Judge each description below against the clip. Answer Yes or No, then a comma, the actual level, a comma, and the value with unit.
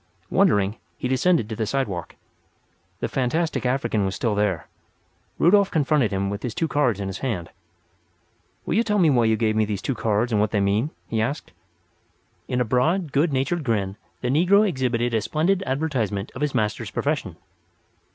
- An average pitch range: No, wide, 5.9 semitones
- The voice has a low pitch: Yes, low, 120 Hz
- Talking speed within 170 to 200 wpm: Yes, average, 180 wpm